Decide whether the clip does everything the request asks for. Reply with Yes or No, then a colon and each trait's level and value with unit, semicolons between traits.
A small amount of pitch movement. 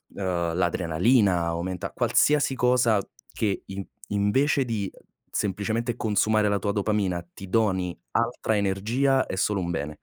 No: average, 3.9 semitones